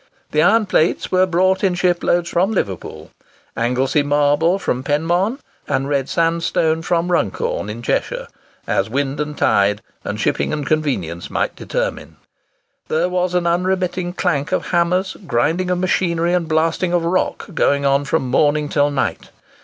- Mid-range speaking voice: Yes, medium, 165 Hz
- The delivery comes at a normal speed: Yes, average, 155 wpm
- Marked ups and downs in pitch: No, average, 3.9 semitones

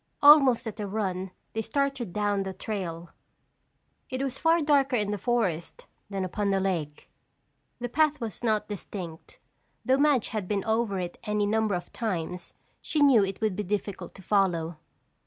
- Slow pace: No, average, 170 wpm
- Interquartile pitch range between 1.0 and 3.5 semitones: No, average, 4.3 semitones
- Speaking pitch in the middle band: No, high, 210 Hz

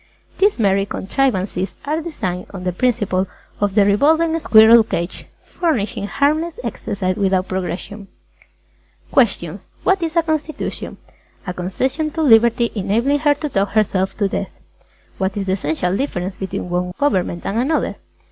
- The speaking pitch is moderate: No, high, 205 Hz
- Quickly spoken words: No, average, 155 wpm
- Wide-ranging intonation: Yes, wide, 7.4 semitones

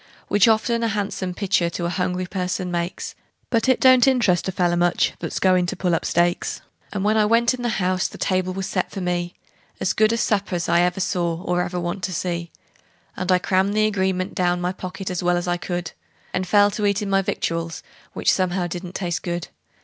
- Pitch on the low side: No, medium, 185 Hz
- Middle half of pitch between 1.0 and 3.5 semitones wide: Yes, narrow, 2.4 semitones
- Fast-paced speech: Yes, fast, 220 wpm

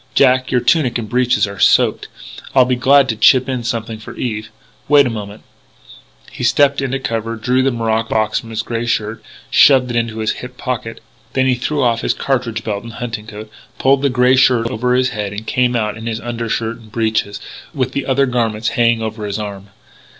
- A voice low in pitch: Yes, low, 115 Hz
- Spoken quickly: Yes, fast, 210 wpm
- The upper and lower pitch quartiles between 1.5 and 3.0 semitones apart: Yes, narrow, 2.5 semitones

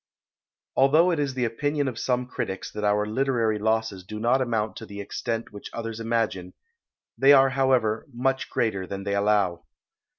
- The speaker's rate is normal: Yes, average, 170 wpm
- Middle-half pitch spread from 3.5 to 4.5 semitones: Yes, average, 4.0 semitones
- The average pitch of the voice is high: No, low, 115 Hz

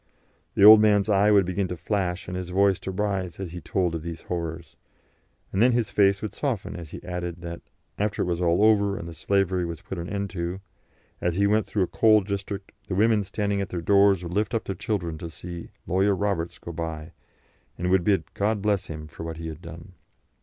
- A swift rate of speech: Yes, fast, 225 wpm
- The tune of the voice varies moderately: Yes, average, 3.0 semitones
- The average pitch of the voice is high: No, very low, 95 Hz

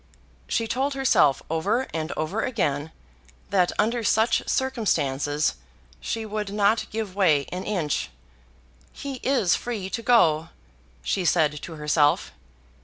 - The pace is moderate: No, slow, 125 wpm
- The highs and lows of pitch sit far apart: Yes, wide, 6.6 semitones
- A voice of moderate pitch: No, high, 195 Hz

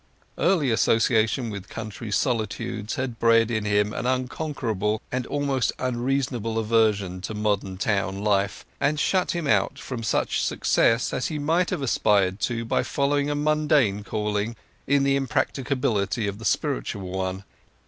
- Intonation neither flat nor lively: Yes, average, 4.7 semitones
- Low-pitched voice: Yes, low, 115 Hz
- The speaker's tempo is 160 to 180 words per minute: No, average, 150 wpm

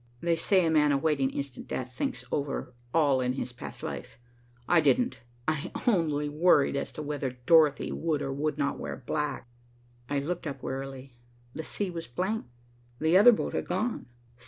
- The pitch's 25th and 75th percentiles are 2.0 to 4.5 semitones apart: Yes, average, 3.4 semitones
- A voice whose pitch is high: No, medium, 150 Hz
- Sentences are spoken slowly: No, average, 170 wpm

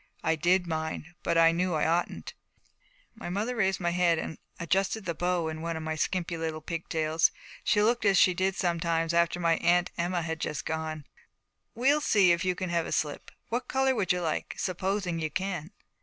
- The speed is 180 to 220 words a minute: Yes, average, 200 wpm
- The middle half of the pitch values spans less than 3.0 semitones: Yes, narrow, 2.5 semitones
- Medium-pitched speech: Yes, medium, 175 Hz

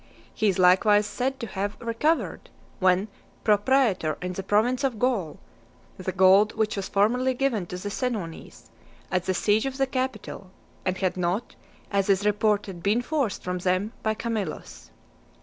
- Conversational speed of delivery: Yes, average, 165 wpm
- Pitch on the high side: Yes, high, 205 Hz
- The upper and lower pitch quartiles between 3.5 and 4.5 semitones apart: Yes, average, 4.1 semitones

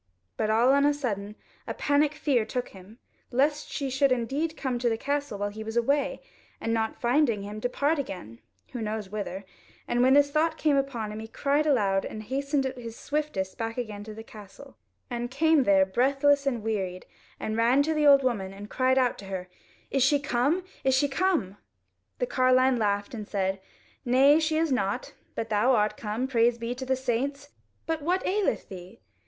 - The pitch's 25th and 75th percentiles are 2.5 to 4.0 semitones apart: No, average, 4.8 semitones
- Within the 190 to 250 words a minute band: Yes, average, 195 wpm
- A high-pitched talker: Yes, high, 245 Hz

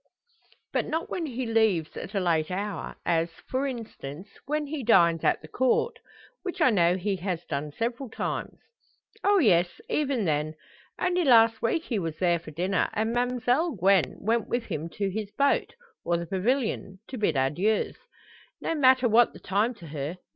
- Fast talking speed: No, average, 175 wpm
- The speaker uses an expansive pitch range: Yes, wide, 6.6 semitones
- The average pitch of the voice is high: Yes, high, 210 Hz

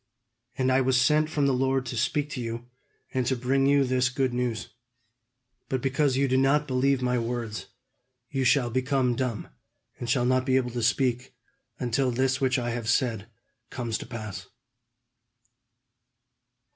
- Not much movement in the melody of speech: Yes, narrow, 1.8 semitones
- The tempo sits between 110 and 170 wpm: Yes, average, 165 wpm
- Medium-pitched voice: No, low, 130 Hz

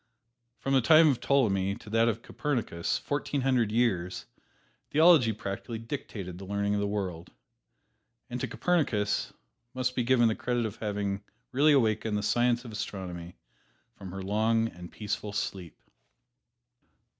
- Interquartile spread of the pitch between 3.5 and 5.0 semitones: Yes, average, 3.9 semitones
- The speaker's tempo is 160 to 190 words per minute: No, average, 145 wpm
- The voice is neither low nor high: No, low, 110 Hz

